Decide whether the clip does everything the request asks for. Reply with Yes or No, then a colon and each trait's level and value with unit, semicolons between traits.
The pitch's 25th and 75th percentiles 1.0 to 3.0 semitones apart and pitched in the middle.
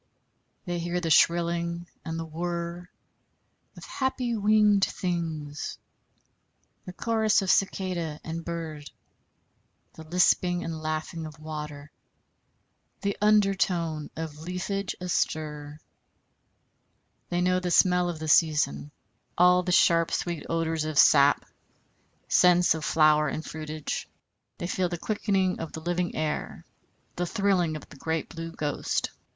Yes: narrow, 2.5 semitones; medium, 170 Hz